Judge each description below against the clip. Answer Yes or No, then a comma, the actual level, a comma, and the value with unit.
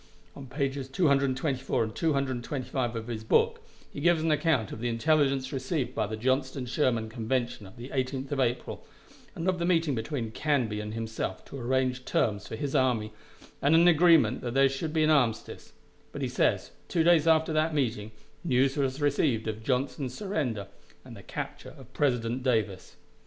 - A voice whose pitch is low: Yes, low, 130 Hz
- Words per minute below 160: No, average, 180 wpm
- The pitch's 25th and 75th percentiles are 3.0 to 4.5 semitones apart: Yes, average, 4.1 semitones